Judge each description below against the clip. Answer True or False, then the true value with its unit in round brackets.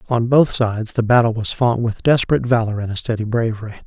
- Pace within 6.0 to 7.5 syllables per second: True (6.5 syllables/s)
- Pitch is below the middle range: True (115 Hz)